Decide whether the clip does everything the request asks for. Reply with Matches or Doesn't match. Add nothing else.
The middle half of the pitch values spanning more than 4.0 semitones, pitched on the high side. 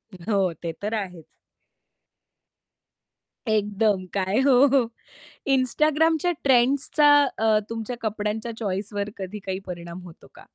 Matches